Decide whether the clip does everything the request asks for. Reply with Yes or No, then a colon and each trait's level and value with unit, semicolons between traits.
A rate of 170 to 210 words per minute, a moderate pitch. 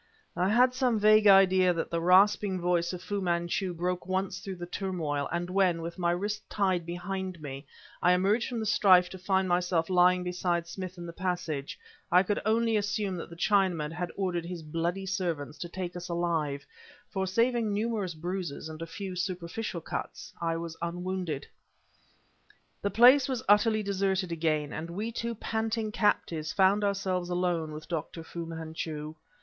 Yes: average, 175 wpm; medium, 180 Hz